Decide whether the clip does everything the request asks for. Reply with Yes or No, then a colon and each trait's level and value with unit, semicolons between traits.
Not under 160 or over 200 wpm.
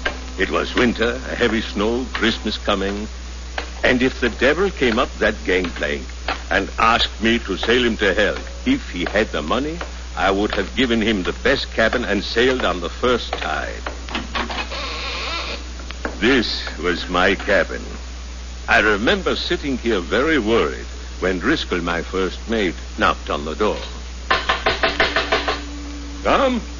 No: average, 140 wpm